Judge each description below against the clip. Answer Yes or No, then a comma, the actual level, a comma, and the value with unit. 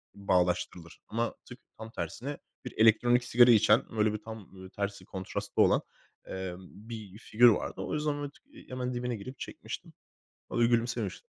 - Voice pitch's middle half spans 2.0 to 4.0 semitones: Yes, average, 3.5 semitones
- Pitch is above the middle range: No, low, 110 Hz